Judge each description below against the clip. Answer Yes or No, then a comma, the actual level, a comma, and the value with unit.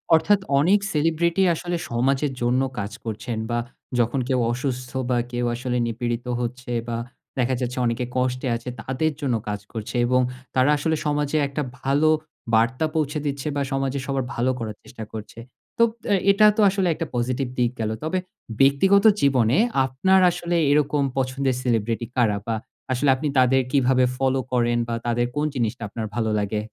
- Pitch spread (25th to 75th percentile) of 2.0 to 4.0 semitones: Yes, average, 3.5 semitones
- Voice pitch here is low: Yes, low, 130 Hz